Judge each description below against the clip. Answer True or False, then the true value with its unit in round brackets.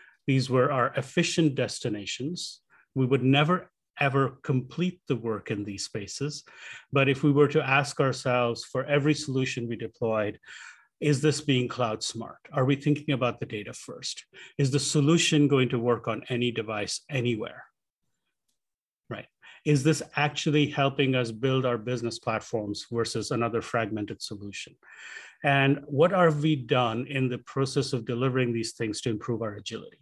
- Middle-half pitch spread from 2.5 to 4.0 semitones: True (3.7 semitones)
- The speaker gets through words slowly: False (160 wpm)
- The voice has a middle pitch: False (130 Hz)